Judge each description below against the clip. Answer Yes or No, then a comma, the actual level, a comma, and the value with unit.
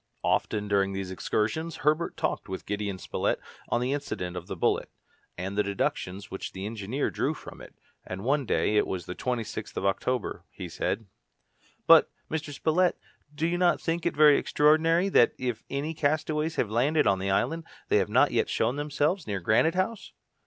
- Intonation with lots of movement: Yes, wide, 7.7 semitones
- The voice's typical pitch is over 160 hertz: No, low, 125 Hz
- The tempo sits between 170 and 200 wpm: Yes, average, 185 wpm